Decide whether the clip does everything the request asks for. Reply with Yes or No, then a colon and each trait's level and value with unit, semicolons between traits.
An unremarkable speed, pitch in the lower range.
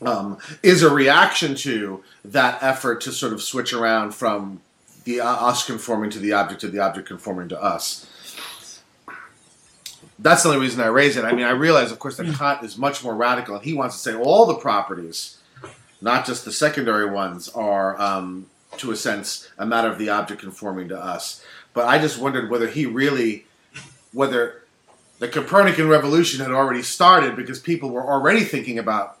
Yes: average, 185 wpm; low, 120 Hz